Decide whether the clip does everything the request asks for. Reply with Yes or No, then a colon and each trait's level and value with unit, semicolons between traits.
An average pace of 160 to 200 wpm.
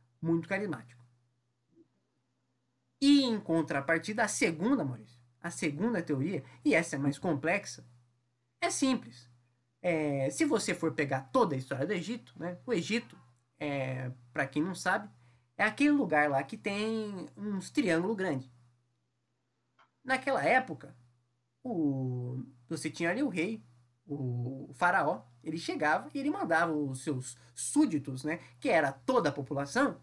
No: average, 140 wpm